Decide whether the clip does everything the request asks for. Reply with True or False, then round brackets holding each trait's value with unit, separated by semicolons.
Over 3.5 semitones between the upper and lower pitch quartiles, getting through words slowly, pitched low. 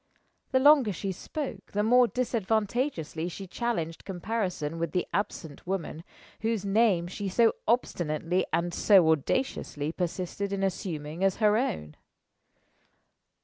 False (5.0 semitones; 125 wpm; 195 Hz)